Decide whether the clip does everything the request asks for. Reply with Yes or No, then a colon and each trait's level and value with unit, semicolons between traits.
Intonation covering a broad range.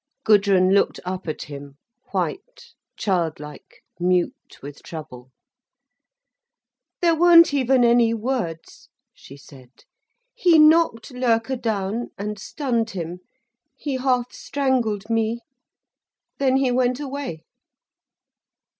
Yes: wide, 6.6 semitones